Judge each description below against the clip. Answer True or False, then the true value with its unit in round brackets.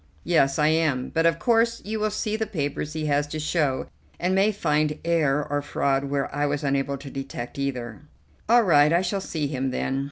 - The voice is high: False (150 Hz)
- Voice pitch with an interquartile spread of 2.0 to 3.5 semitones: False (4.0 semitones)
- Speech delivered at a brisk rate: True (210 wpm)